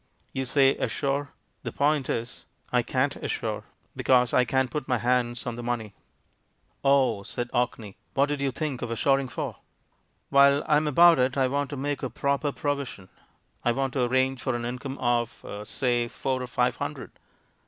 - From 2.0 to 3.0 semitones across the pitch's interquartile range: Yes, narrow, 2.4 semitones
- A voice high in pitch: No, low, 130 Hz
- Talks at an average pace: Yes, average, 180 wpm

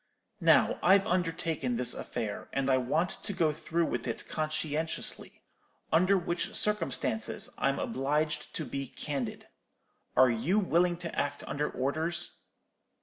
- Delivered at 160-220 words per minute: No, slow, 135 wpm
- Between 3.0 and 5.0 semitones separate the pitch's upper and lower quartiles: Yes, average, 4.3 semitones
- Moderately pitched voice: Yes, medium, 155 Hz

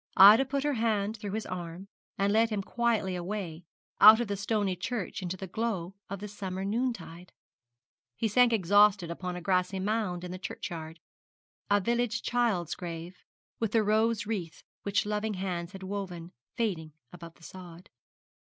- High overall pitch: Yes, high, 200 Hz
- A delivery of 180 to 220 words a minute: No, average, 165 wpm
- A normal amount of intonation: Yes, average, 3.5 semitones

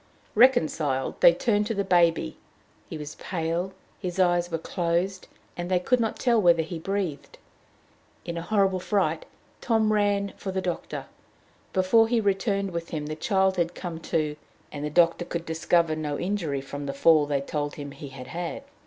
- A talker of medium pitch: Yes, medium, 175 Hz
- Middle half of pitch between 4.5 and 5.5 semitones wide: No, average, 4.0 semitones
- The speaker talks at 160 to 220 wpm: Yes, average, 180 wpm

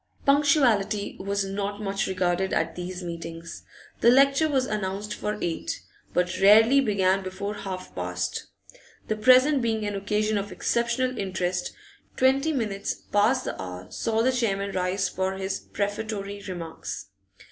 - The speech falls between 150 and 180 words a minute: No, average, 140 wpm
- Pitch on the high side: Yes, high, 200 Hz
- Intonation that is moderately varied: Yes, average, 3.5 semitones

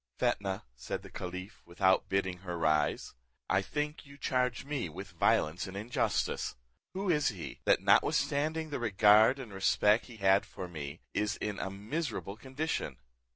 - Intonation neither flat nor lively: No, wide, 6.2 semitones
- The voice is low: Yes, low, 100 Hz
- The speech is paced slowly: No, average, 155 wpm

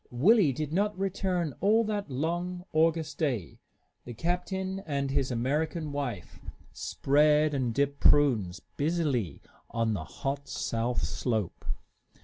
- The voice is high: No, medium, 145 Hz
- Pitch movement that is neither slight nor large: No, wide, 5.8 semitones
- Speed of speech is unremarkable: No, slow, 125 wpm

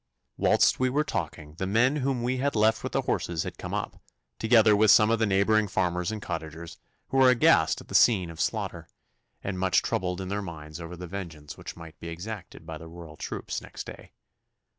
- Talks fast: Yes, fast, 210 wpm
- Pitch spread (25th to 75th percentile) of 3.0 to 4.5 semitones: No, average, 5.0 semitones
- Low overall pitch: Yes, very low, 95 Hz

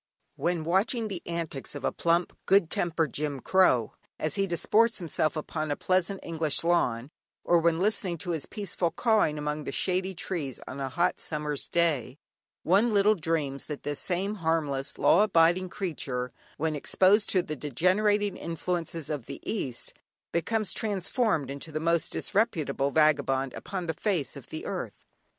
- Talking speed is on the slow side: No, average, 160 wpm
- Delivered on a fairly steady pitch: No, average, 4.2 semitones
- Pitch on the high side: No, medium, 165 Hz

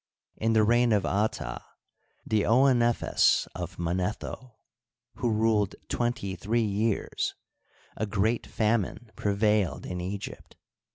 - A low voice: Yes, low, 110 Hz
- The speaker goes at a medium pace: No, slow, 110 wpm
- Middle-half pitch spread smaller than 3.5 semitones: Yes, average, 2.7 semitones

